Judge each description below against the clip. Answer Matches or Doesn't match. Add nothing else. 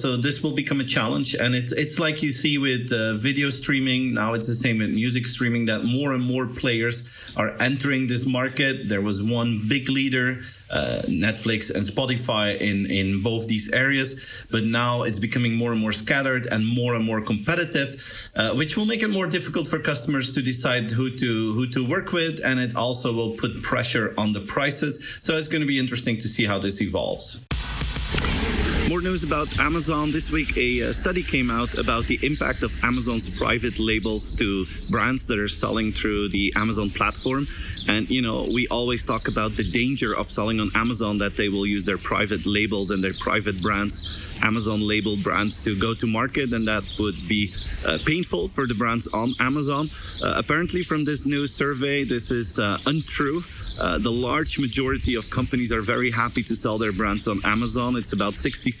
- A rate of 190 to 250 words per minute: Matches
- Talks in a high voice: Doesn't match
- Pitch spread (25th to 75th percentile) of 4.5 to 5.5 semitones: Doesn't match